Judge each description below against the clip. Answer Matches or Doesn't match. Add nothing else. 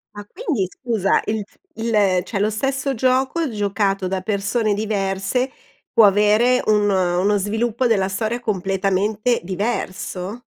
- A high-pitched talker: Matches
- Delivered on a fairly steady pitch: Doesn't match